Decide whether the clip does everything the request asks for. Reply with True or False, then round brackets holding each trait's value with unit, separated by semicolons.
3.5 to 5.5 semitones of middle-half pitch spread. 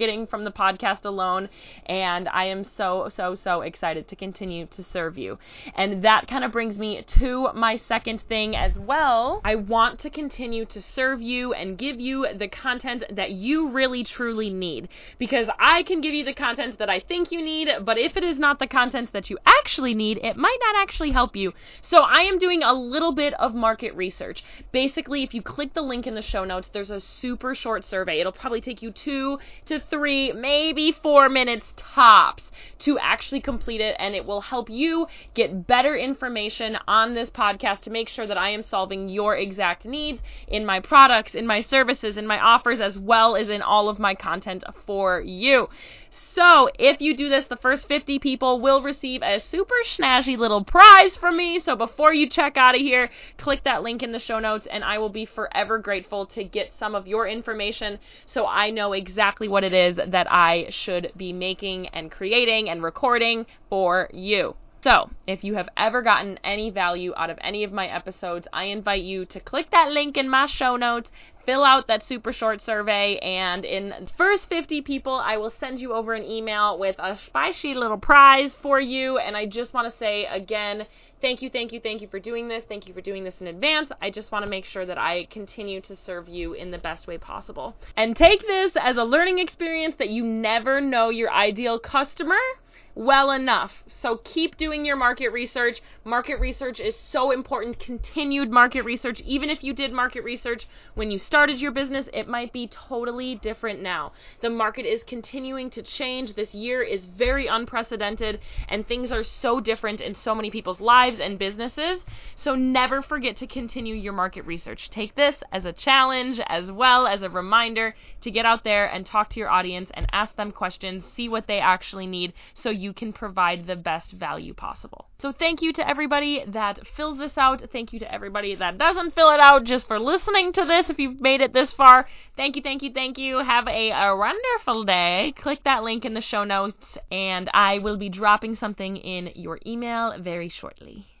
True (5.1 semitones)